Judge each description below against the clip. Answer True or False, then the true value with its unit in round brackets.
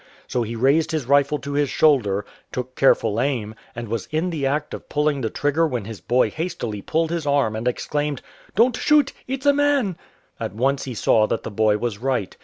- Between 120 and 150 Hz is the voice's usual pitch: True (135 Hz)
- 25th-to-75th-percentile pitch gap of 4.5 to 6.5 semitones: True (5.5 semitones)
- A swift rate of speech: True (220 wpm)